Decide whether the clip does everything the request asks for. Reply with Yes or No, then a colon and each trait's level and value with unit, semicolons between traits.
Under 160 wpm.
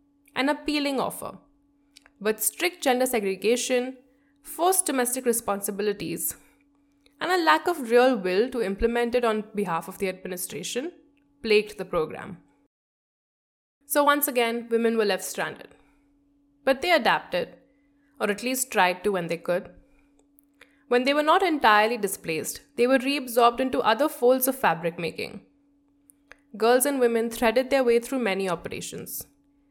Yes: average, 140 wpm